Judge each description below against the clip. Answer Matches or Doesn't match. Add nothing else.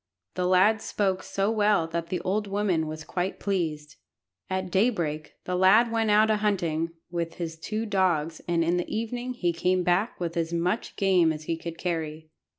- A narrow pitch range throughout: Doesn't match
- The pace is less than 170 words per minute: Doesn't match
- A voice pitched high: Doesn't match